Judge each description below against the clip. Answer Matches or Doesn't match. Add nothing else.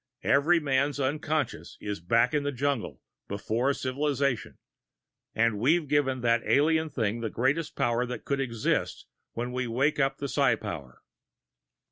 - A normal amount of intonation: Matches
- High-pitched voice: Doesn't match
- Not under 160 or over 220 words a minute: Doesn't match